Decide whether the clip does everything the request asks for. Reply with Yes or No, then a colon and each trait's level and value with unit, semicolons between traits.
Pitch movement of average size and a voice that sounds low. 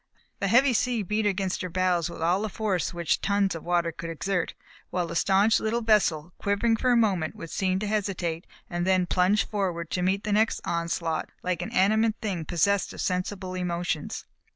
No: average, 3.2 semitones; medium, 185 Hz